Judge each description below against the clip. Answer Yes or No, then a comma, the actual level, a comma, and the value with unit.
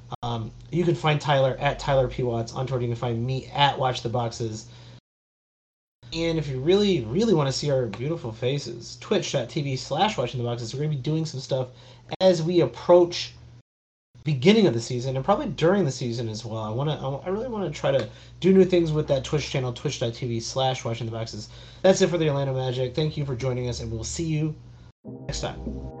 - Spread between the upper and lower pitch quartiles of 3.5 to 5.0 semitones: Yes, average, 4.6 semitones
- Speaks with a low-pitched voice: Yes, low, 130 Hz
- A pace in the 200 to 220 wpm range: Yes, fast, 205 wpm